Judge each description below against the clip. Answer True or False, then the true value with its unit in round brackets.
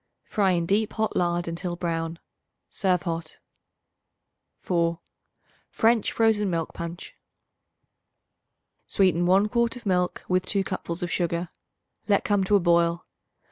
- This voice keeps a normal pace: False (130 wpm)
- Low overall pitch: False (180 Hz)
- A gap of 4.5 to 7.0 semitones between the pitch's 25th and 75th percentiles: False (3.1 semitones)